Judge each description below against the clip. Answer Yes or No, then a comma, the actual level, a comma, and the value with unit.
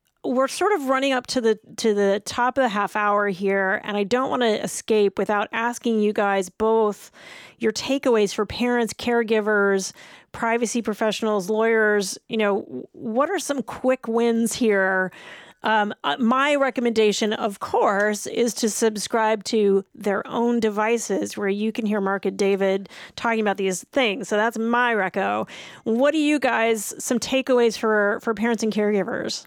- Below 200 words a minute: Yes, average, 165 wpm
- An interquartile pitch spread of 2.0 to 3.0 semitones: Yes, narrow, 2.6 semitones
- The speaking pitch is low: No, high, 220 Hz